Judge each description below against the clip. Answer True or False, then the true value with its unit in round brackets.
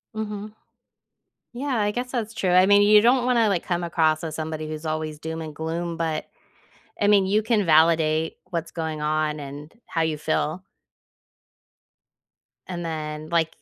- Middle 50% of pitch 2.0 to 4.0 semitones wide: False (4.7 semitones)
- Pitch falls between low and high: True (165 Hz)